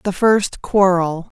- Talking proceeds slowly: Yes, slow, 130 wpm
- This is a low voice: No, medium, 185 Hz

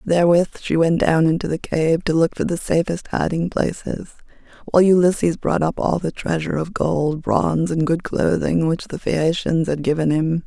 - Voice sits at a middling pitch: Yes, medium, 165 Hz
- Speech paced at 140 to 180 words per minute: No, average, 190 wpm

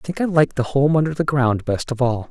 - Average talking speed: No, fast, 310 wpm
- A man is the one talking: Yes, male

